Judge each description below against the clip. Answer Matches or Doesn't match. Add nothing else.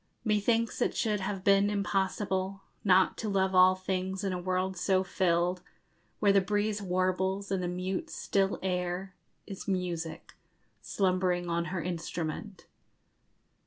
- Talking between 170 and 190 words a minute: Doesn't match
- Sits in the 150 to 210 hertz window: Matches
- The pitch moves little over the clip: Matches